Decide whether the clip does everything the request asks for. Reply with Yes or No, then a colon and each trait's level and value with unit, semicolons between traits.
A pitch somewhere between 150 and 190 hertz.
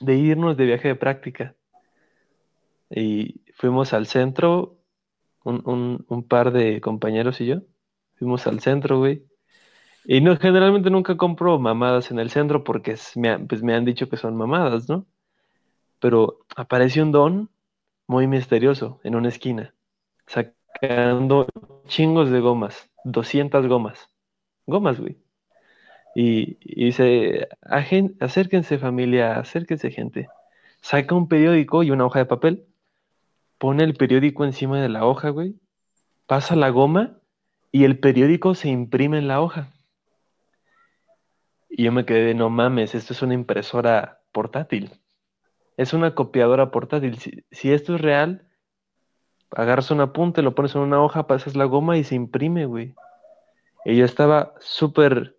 No: medium, 140 Hz